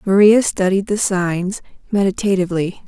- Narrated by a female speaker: Yes, female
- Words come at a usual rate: No, slow, 105 wpm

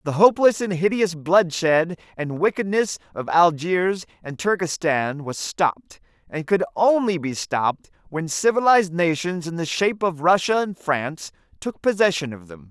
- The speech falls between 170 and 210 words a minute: No, average, 150 wpm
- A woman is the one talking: No, male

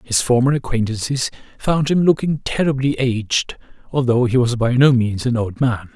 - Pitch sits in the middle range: No, low, 125 Hz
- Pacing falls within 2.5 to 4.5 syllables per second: No, 4.9 syllables/s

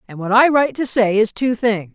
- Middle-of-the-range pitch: No, high, 225 Hz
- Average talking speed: No, fast, 275 wpm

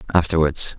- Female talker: No, male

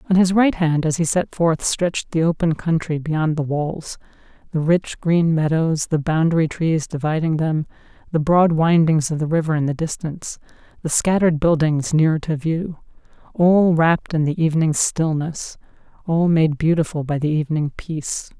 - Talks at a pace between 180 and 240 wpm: No, average, 165 wpm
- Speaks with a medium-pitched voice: Yes, medium, 160 Hz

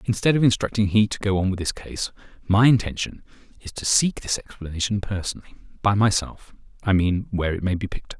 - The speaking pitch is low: Yes, low, 100 Hz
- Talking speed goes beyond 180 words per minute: Yes, average, 190 wpm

